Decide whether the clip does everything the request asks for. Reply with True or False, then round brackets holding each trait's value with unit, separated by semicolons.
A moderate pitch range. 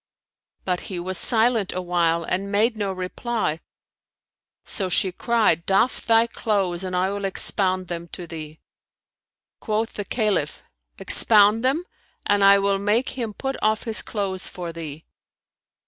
True (3.4 semitones)